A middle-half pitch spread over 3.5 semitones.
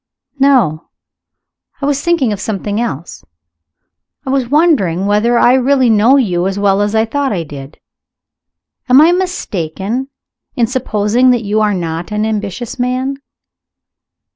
Yes: average, 4.9 semitones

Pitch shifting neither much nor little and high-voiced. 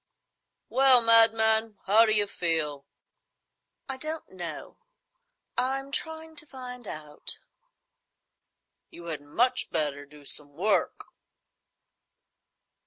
No: wide, 8.7 semitones; high, 220 Hz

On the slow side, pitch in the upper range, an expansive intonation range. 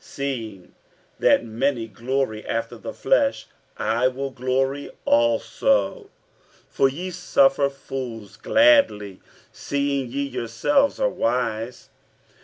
No: slow, 110 wpm; low, 135 Hz; wide, 6.4 semitones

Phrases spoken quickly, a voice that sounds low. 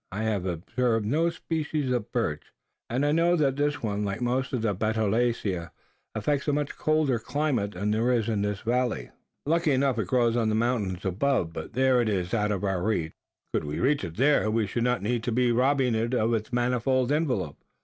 Yes: fast, 210 wpm; low, 120 Hz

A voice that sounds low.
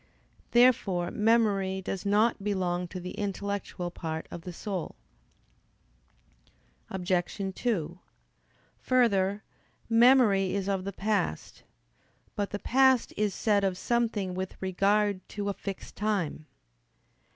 No: high, 200 Hz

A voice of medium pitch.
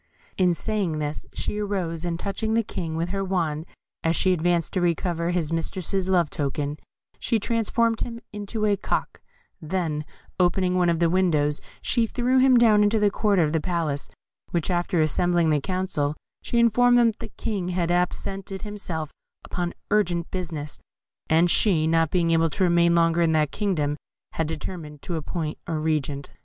Yes: medium, 175 Hz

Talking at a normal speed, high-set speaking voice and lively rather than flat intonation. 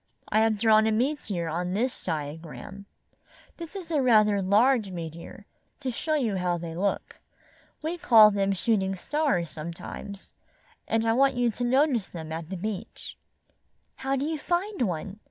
Yes: average, 160 wpm; high, 215 Hz; wide, 6.4 semitones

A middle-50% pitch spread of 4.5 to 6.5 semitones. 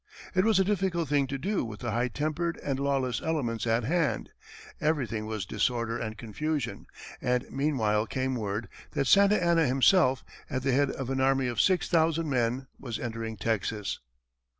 Yes: average, 5.3 semitones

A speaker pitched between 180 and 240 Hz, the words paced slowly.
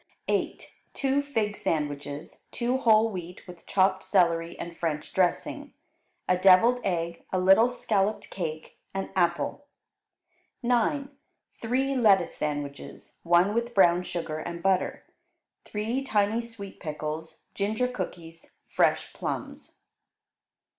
Yes: high, 190 Hz; slow, 115 wpm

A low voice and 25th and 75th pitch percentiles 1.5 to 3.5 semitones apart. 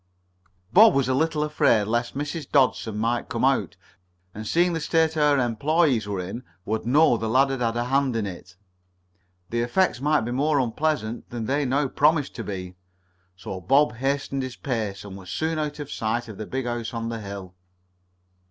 No: low, 125 Hz; average, 4.9 semitones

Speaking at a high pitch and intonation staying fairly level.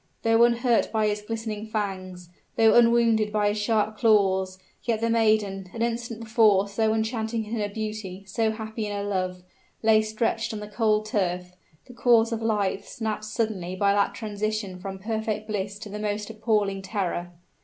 Yes: high, 215 Hz; narrow, 1.8 semitones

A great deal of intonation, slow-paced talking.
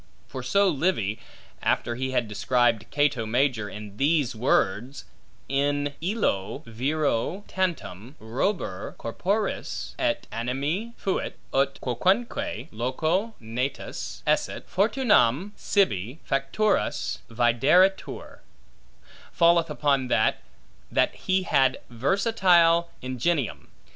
Yes: wide, 7.4 semitones; slow, 95 wpm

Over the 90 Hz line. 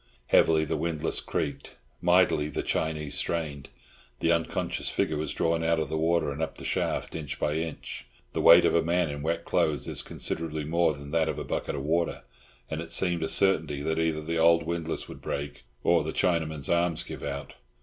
No: very low, 80 Hz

